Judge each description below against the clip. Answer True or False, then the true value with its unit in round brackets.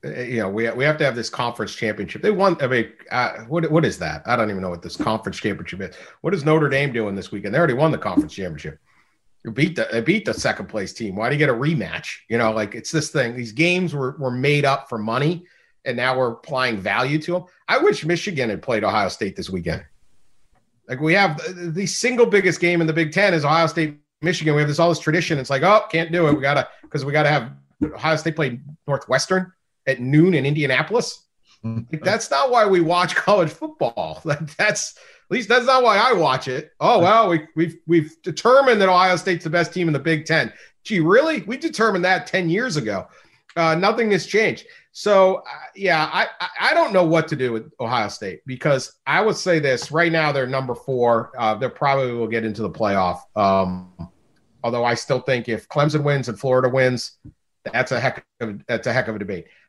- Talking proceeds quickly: True (230 wpm)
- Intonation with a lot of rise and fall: True (6.4 semitones)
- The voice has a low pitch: False (155 Hz)